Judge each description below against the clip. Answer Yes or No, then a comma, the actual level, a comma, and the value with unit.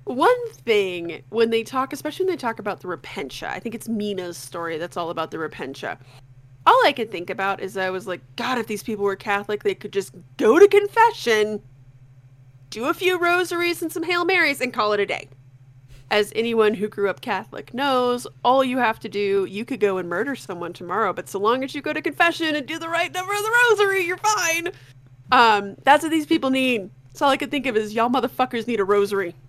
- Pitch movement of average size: No, wide, 7.9 semitones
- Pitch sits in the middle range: No, high, 220 Hz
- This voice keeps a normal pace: No, fast, 220 wpm